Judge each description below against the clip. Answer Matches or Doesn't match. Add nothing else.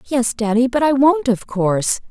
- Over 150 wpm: Matches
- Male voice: Doesn't match